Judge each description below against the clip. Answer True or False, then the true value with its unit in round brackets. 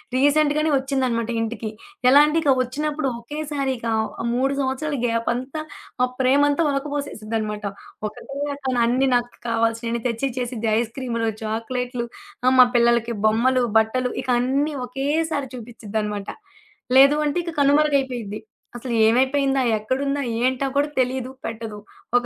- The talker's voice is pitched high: True (255 Hz)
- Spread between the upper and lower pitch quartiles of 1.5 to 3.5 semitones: True (3.2 semitones)